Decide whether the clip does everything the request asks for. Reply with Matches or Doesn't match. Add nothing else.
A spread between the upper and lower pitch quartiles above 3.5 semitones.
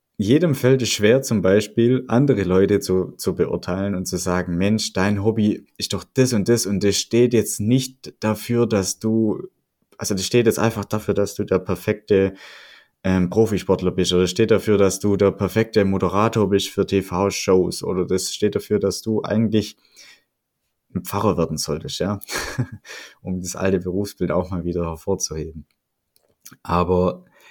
Doesn't match